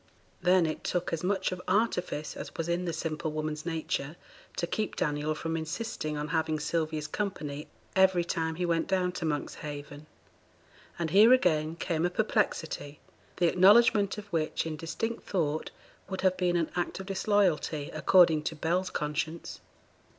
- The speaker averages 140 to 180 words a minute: Yes, average, 160 wpm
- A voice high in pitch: No, medium, 165 Hz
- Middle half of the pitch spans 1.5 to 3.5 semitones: Yes, average, 3.2 semitones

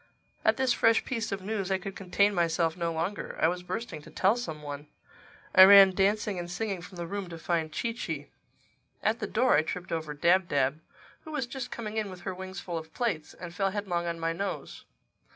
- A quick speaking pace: Yes, fast, 220 wpm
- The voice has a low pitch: No, medium, 185 Hz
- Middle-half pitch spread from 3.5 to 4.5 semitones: Yes, average, 3.8 semitones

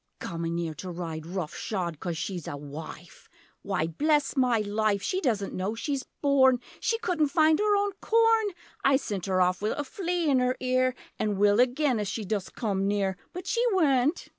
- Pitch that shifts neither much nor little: No, wide, 7.8 semitones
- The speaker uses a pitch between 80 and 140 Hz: No, high, 220 Hz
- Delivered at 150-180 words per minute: No, average, 190 wpm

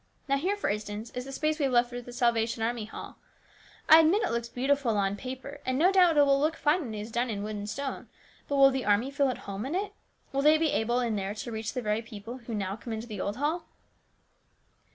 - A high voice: Yes, high, 245 Hz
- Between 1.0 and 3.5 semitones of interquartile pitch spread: No, average, 4.5 semitones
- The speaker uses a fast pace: Yes, fast, 255 wpm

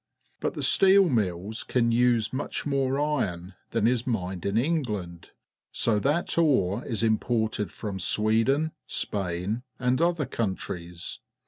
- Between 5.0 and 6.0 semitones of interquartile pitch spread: Yes, wide, 5.4 semitones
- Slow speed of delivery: Yes, slow, 130 wpm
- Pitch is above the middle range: No, low, 115 Hz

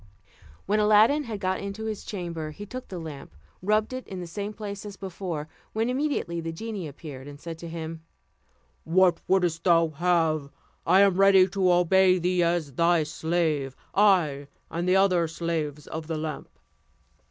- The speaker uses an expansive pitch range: No, average, 3.6 semitones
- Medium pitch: Yes, medium, 175 Hz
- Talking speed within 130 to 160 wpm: No, average, 170 wpm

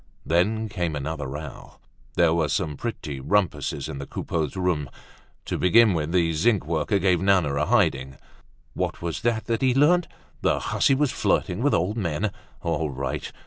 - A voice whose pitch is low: Yes, very low, 85 Hz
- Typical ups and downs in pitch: No, wide, 6.1 semitones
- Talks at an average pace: Yes, average, 165 wpm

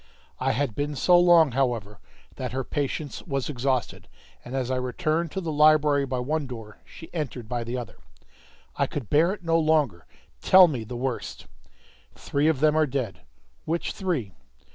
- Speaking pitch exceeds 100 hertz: Yes, medium, 140 Hz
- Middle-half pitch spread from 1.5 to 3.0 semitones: No, average, 4.1 semitones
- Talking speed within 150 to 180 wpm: Yes, average, 175 wpm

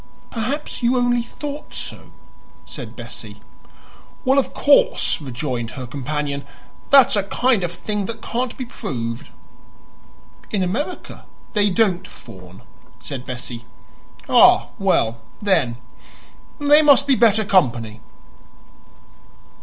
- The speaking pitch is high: Yes, high, 200 Hz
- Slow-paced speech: Yes, slow, 115 wpm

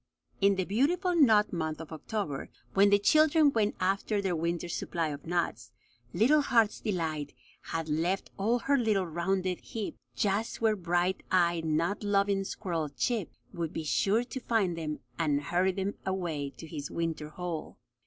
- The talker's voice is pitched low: No, medium, 185 Hz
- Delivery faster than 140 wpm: Yes, average, 165 wpm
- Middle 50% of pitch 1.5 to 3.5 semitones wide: No, average, 4.3 semitones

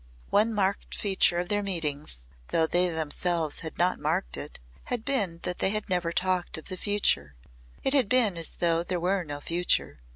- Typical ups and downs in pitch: Yes, average, 3.3 semitones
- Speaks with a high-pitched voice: No, medium, 180 Hz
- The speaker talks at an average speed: Yes, average, 190 wpm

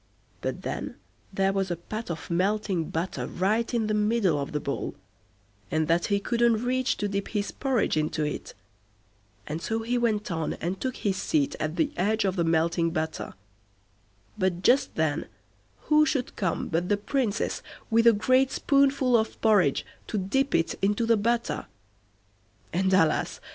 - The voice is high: Yes, high, 205 Hz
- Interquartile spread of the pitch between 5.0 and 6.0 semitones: Yes, wide, 5.5 semitones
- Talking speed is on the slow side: No, average, 170 wpm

